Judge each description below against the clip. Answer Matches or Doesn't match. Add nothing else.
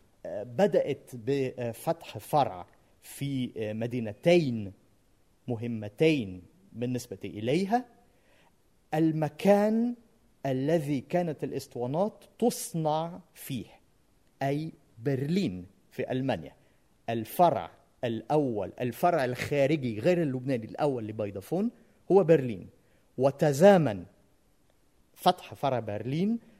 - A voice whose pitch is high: Doesn't match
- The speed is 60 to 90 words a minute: Matches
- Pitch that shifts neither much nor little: Doesn't match